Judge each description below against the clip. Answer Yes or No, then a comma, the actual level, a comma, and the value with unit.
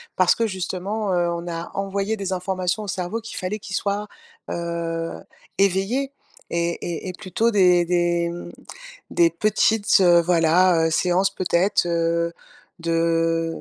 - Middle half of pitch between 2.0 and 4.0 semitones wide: Yes, narrow, 2.6 semitones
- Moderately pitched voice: Yes, medium, 180 Hz